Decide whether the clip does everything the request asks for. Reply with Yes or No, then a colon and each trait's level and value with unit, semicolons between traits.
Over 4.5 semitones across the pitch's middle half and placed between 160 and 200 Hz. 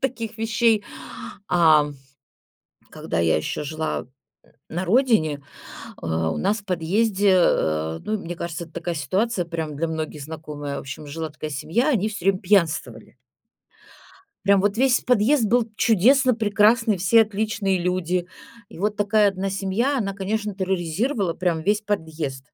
Yes: average, 5.2 semitones; high, 190 Hz